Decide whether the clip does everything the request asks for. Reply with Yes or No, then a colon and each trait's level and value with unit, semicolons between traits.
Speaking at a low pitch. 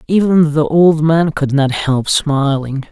No: medium, 150 Hz